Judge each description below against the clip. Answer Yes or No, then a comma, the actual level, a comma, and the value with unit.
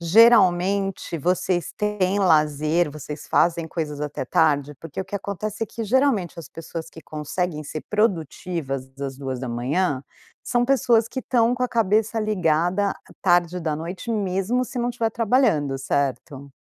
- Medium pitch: Yes, medium, 180 Hz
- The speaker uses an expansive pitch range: Yes, wide, 5.9 semitones